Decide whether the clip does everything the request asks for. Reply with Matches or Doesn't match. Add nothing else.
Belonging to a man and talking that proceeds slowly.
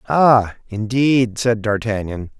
Matches